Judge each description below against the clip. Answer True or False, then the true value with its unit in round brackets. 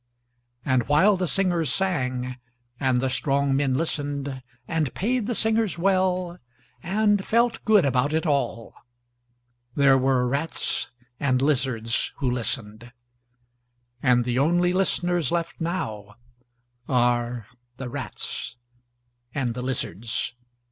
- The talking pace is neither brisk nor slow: False (110 wpm)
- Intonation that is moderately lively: False (5.9 semitones)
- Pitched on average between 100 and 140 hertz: True (135 Hz)